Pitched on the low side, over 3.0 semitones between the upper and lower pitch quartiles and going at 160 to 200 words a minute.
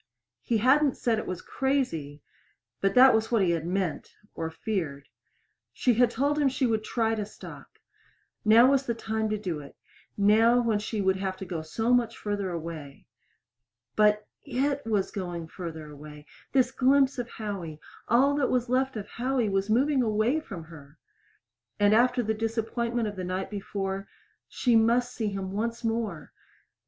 No: high, 215 Hz; average, 4.4 semitones; average, 170 wpm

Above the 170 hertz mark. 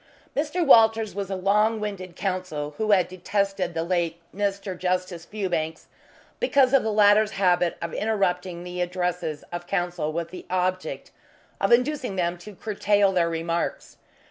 Yes: medium, 185 Hz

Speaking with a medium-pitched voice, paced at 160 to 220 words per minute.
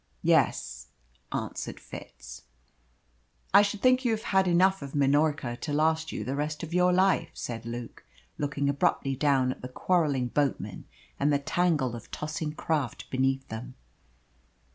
No: medium, 145 Hz; average, 150 wpm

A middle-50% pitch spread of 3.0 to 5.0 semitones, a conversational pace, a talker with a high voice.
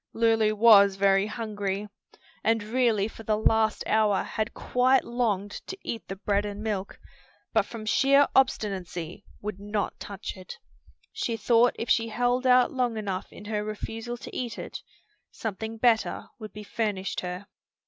No: narrow, 2.4 semitones; average, 160 wpm; high, 215 Hz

